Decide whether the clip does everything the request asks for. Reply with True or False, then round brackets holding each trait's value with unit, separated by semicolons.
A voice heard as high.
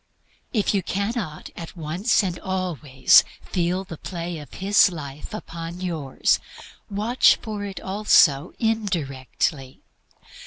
False (180 Hz)